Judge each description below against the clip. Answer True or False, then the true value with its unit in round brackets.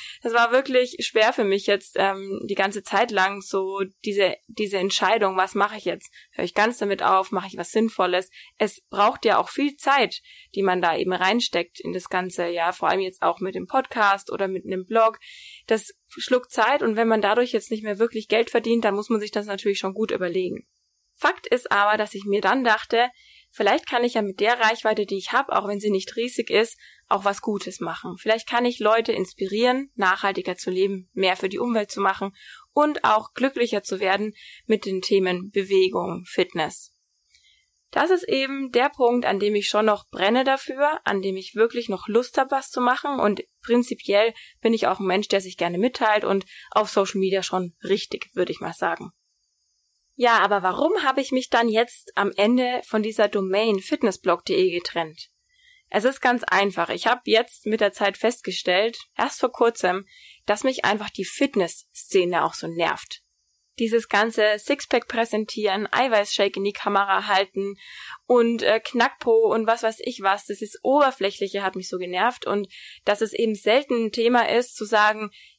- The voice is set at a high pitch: True (215 Hz)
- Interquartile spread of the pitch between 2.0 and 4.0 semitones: True (3.6 semitones)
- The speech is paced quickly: True (195 wpm)